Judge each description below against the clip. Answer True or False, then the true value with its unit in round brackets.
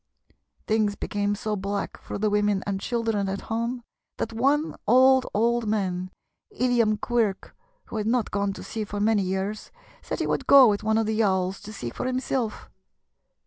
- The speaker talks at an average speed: True (180 wpm)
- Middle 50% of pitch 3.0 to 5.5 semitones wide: False (2.5 semitones)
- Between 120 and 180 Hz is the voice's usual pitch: False (215 Hz)